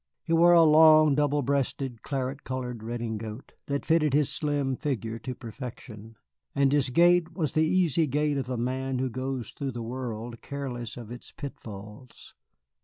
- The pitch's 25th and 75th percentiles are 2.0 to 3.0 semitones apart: No, average, 3.6 semitones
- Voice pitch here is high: No, low, 130 Hz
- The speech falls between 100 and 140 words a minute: No, average, 165 wpm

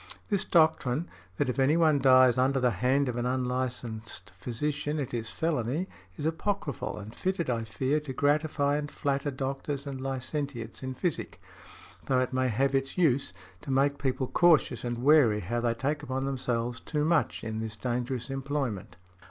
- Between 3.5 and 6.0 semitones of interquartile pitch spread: No, average, 3.1 semitones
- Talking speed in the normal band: Yes, average, 170 wpm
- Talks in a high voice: No, low, 135 Hz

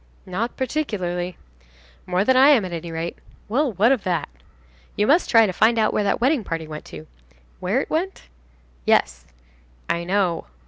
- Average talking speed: Yes, average, 175 wpm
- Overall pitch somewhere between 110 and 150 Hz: No, high, 200 Hz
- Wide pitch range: Yes, wide, 6.4 semitones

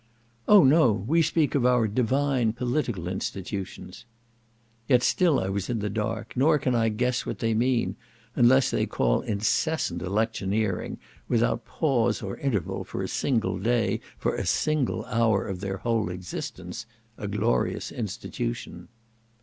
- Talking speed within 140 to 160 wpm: Yes, average, 145 wpm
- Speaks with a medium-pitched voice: No, low, 115 Hz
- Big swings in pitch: No, average, 4.3 semitones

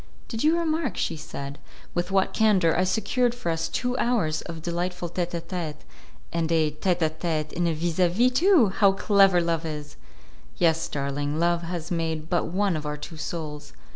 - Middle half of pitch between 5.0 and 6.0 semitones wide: No, average, 3.4 semitones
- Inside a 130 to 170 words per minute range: No, average, 195 wpm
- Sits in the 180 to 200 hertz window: No, medium, 170 Hz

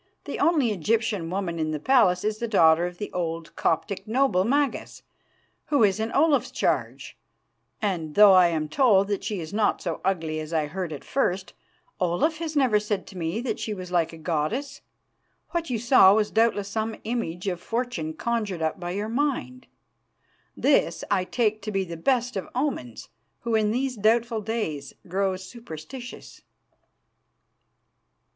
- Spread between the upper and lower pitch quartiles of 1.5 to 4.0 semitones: No, average, 5.2 semitones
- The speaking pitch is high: Yes, high, 205 Hz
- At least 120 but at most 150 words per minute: No, average, 165 wpm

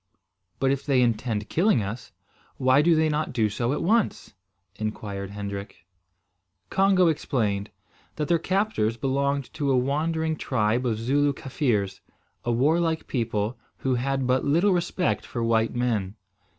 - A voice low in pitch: Yes, low, 130 Hz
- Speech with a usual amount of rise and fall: No, wide, 5.7 semitones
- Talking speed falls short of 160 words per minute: Yes, average, 145 wpm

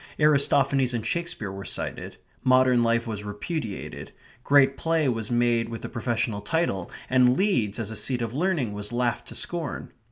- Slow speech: No, average, 165 wpm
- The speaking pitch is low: Yes, low, 120 Hz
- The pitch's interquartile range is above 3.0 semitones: Yes, average, 4.0 semitones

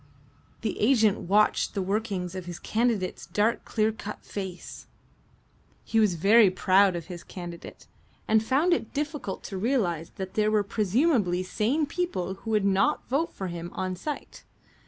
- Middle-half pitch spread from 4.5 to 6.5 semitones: No, average, 3.7 semitones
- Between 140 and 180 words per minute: Yes, average, 155 wpm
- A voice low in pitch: No, high, 205 Hz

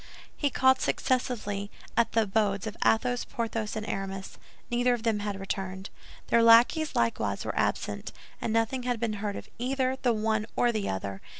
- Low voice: No, high, 225 Hz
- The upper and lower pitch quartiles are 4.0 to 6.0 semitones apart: No, average, 3.3 semitones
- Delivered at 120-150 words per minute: No, average, 175 wpm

